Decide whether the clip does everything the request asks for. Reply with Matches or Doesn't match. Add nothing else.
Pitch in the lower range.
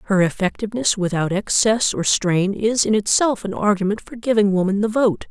Doesn't match